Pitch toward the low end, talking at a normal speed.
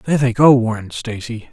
Yes: low, 120 Hz; average, 195 wpm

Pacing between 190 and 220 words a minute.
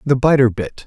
Yes: fast, 210 wpm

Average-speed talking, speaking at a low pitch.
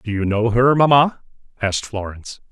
Yes: average, 165 wpm; low, 120 Hz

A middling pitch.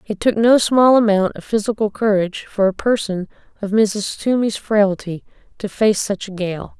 No: high, 205 Hz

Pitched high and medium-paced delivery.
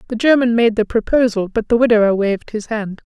No: high, 220 Hz; fast, 210 wpm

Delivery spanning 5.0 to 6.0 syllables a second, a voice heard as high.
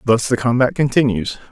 No: 5.6 syllables/s; low, 120 Hz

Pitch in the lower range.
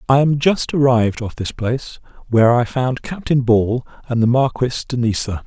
Yes: low, 125 Hz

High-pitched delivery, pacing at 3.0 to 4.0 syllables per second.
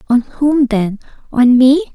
Yes: very high, 255 Hz; 3.7 syllables/s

